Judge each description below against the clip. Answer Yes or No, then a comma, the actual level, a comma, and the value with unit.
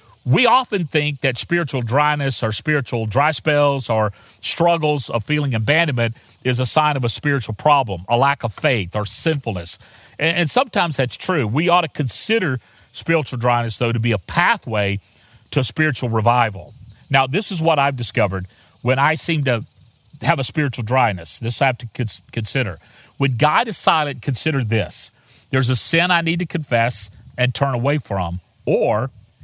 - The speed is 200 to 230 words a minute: No, average, 170 wpm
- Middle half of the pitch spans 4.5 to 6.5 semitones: Yes, average, 5.1 semitones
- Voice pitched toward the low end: Yes, low, 125 Hz